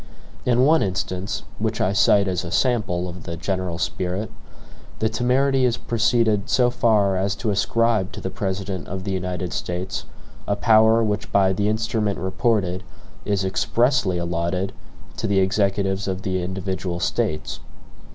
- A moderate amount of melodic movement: Yes, average, 3.1 semitones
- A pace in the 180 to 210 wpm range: No, average, 150 wpm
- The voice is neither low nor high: No, low, 100 Hz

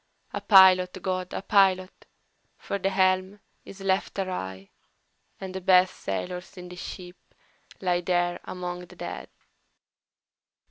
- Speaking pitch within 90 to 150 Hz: No, medium, 185 Hz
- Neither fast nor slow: No, slow, 130 wpm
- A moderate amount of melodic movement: No, narrow, 1.0 semitones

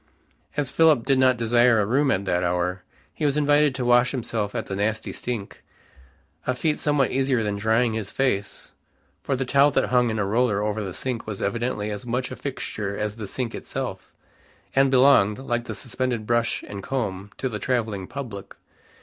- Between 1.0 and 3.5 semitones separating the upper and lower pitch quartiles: No, average, 4.1 semitones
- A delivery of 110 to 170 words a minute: No, average, 190 wpm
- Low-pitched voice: Yes, low, 120 Hz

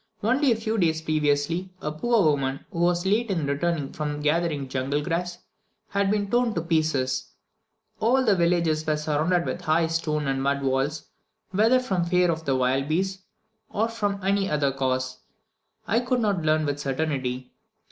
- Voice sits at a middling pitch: Yes, medium, 160 Hz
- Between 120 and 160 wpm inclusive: No, average, 170 wpm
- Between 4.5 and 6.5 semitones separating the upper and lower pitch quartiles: Yes, average, 5.2 semitones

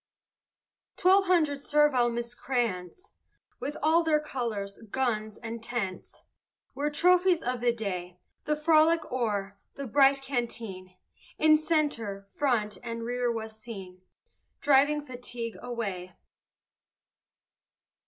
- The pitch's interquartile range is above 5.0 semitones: Yes, wide, 5.4 semitones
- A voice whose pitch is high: Yes, high, 245 Hz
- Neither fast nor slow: No, slow, 105 wpm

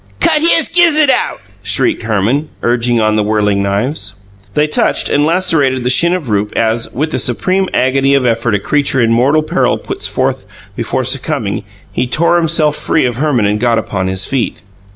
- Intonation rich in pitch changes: Yes, wide, 5.8 semitones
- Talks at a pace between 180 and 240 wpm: Yes, average, 185 wpm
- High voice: No, low, 130 Hz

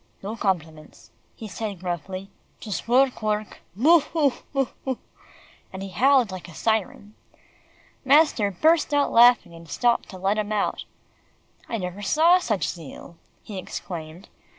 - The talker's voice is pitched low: No, high, 210 Hz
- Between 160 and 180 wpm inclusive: No, average, 145 wpm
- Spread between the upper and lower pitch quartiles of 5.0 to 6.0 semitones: Yes, wide, 5.4 semitones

